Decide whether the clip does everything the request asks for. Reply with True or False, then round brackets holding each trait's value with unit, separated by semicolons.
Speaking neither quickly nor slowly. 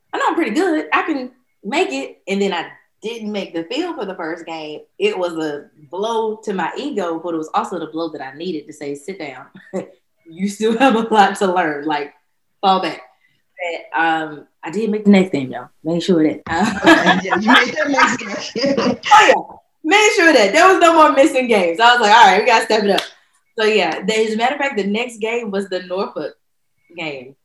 False (215 wpm)